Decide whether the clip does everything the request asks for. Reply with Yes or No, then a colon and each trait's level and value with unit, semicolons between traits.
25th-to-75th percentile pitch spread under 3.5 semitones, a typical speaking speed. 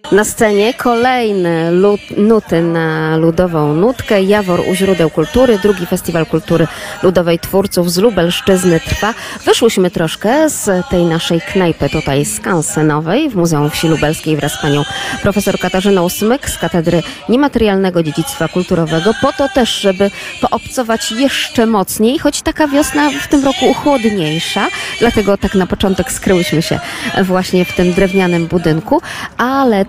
No: average, 4.9 semitones; average, 140 wpm